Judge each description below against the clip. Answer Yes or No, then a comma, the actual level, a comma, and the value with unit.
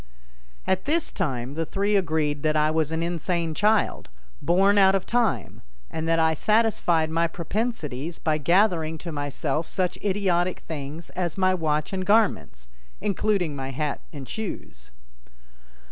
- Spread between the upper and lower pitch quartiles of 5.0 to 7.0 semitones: No, average, 4.1 semitones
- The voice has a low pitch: No, medium, 165 Hz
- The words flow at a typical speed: Yes, average, 145 wpm